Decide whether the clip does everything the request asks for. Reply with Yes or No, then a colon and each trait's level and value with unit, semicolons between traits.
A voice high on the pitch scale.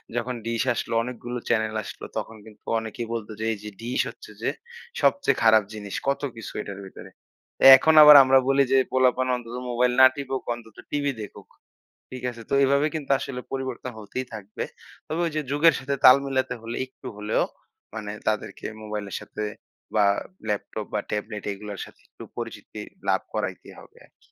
No: low, 120 Hz